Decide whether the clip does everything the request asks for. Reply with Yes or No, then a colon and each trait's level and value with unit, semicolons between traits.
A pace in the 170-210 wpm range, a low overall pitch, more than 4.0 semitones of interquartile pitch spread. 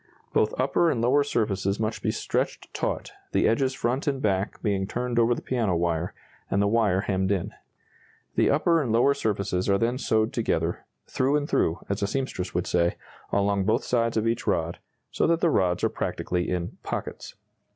Yes: average, 190 wpm; low, 110 Hz; average, 4.7 semitones